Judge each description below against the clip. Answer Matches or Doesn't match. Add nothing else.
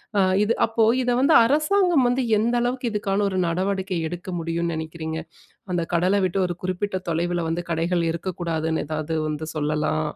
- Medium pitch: Matches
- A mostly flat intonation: Doesn't match